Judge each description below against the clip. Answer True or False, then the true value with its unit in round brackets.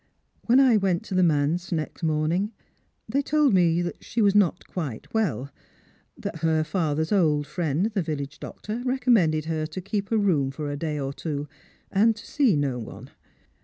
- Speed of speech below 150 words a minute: False (185 wpm)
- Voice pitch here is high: False (170 Hz)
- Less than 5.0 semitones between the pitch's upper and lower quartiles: False (5.4 semitones)